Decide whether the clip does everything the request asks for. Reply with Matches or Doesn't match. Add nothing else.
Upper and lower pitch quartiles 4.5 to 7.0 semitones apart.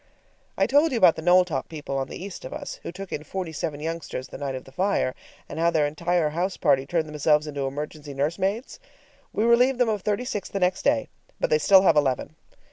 Matches